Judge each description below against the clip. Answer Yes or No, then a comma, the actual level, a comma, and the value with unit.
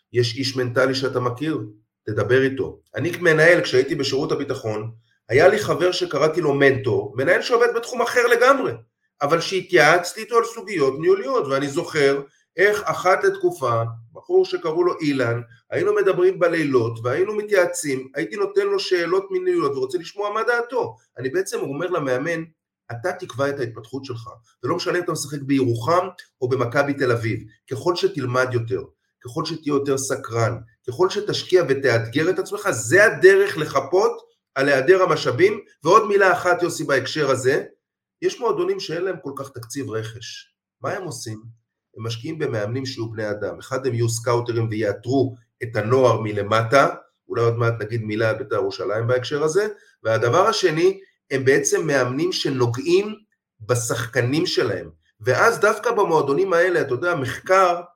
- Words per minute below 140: No, fast, 150 wpm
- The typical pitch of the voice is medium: Yes, medium, 155 Hz